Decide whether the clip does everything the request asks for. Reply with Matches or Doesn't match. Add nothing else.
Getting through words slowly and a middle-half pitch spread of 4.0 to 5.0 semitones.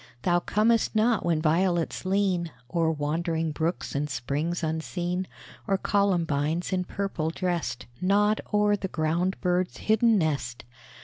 Doesn't match